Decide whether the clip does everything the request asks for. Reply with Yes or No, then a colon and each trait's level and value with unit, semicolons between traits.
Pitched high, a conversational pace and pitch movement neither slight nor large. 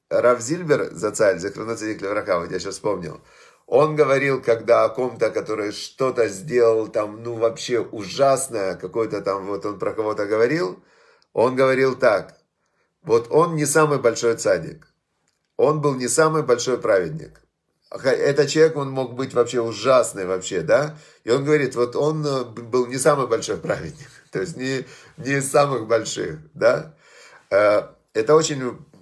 No: low, 130 Hz; average, 150 wpm; average, 4.4 semitones